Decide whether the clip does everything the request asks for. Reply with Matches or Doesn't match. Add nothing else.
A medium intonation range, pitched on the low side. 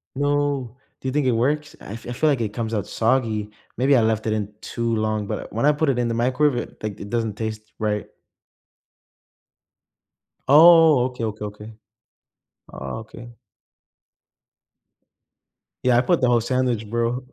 Matches